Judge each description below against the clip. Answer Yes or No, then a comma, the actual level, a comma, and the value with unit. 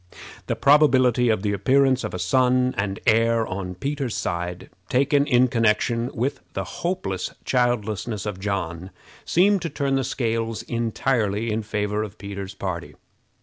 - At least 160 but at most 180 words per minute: No, average, 145 wpm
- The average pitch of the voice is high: No, low, 115 Hz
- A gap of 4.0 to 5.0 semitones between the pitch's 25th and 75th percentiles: Yes, average, 4.4 semitones